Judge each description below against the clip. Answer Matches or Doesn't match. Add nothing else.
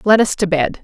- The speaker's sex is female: Matches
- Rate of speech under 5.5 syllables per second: Doesn't match